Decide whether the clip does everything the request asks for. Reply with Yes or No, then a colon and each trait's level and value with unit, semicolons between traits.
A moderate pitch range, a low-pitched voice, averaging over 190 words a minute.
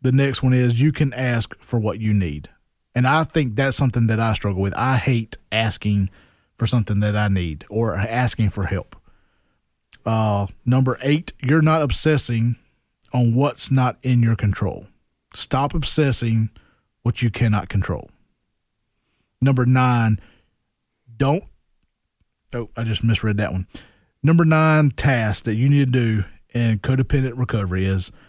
No: average, 4.1 semitones; low, 115 Hz; average, 150 wpm